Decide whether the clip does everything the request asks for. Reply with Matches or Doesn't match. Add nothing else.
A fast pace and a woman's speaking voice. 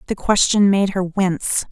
Doesn't match